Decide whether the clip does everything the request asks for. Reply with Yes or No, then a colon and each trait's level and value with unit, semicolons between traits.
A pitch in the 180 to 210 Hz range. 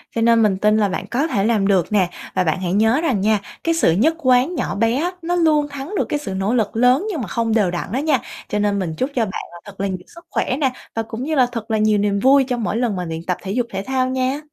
No: high, 225 Hz